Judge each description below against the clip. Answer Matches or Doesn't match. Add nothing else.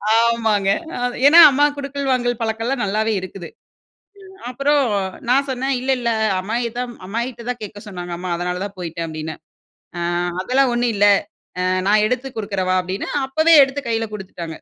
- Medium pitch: Doesn't match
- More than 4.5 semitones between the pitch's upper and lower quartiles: Matches